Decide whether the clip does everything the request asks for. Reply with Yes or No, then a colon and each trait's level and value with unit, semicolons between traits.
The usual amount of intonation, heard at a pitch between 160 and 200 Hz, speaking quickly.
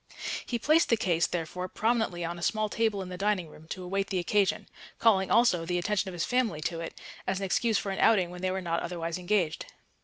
Yes: average, 3.3 semitones; medium, 185 Hz; fast, 235 wpm